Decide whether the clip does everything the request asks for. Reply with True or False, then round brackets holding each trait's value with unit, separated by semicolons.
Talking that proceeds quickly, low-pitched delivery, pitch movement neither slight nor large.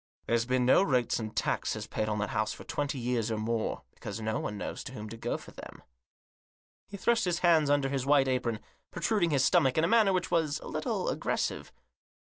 False (220 wpm; 130 Hz; 6.2 semitones)